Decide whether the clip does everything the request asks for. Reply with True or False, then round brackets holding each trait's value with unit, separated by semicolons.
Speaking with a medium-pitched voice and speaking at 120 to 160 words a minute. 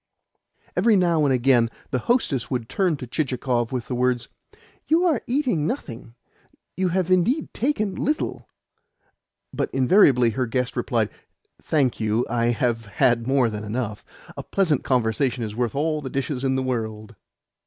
False (130 Hz; 155 wpm)